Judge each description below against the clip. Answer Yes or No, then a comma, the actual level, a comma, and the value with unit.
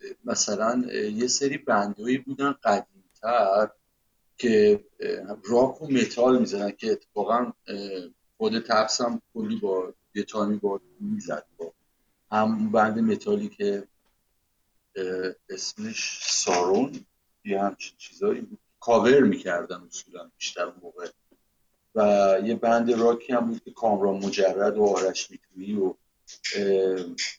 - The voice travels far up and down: Yes, wide, 6.1 semitones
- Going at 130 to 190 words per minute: No, slow, 105 wpm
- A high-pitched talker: No, low, 110 Hz